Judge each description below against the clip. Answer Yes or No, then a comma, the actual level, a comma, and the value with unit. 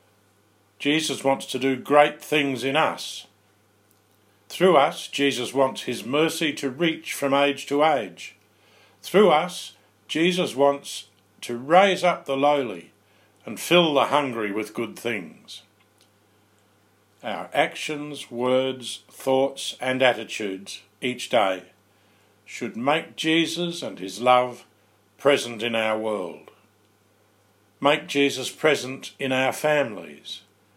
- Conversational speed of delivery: No, slow, 115 wpm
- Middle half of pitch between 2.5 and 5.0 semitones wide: No, wide, 5.5 semitones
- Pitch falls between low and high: No, low, 125 Hz